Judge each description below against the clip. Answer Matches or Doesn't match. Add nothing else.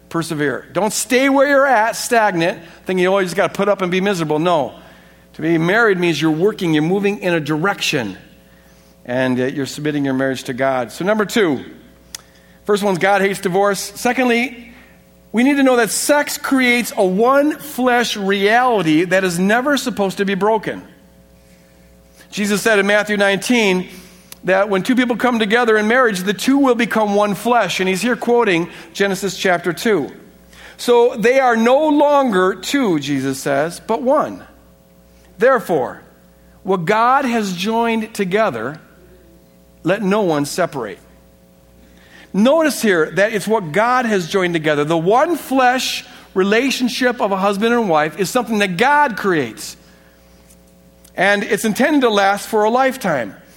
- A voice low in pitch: Doesn't match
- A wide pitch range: Matches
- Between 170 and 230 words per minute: Doesn't match